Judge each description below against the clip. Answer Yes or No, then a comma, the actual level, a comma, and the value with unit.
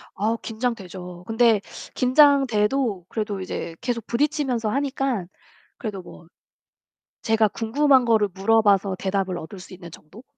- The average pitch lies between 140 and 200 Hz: No, high, 220 Hz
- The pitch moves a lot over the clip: No, average, 4.5 semitones